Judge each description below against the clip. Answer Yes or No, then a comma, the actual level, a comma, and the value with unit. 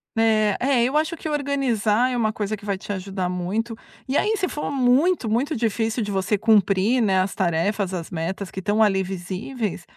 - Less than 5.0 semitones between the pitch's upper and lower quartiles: Yes, average, 4.5 semitones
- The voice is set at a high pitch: Yes, high, 215 Hz